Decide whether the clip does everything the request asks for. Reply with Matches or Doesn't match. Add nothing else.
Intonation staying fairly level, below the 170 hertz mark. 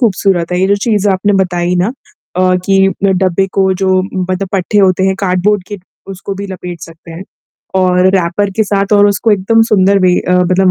Doesn't match